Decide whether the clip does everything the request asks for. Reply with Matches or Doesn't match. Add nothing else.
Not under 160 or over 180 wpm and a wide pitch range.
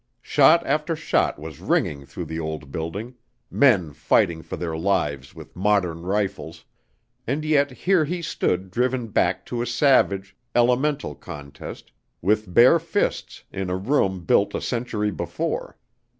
Doesn't match